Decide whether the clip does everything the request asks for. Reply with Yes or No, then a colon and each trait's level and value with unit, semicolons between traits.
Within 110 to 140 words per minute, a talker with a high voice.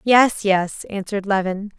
Yes: slow, 135 wpm; high, 200 Hz